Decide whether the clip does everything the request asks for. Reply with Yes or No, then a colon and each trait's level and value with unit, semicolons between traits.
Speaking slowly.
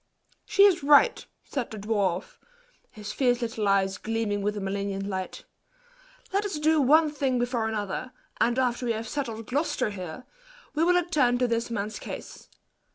No: average, 165 wpm